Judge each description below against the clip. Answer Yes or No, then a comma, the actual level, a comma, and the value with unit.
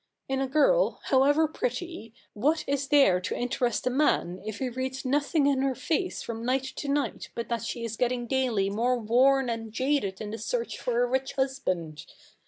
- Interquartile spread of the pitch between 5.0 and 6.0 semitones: No, average, 3.3 semitones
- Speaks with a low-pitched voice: No, very high, 260 Hz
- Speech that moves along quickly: No, average, 190 wpm